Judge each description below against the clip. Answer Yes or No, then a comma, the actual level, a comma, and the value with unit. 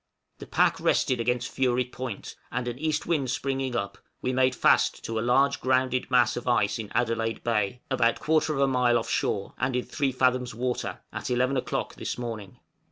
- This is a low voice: Yes, low, 125 Hz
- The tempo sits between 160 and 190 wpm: Yes, average, 185 wpm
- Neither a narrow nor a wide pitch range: No, narrow, 1.6 semitones